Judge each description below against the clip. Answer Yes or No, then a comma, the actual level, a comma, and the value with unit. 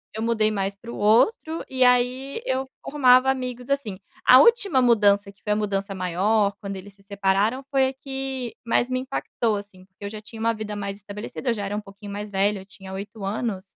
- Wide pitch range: No, average, 4.2 semitones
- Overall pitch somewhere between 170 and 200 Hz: No, high, 215 Hz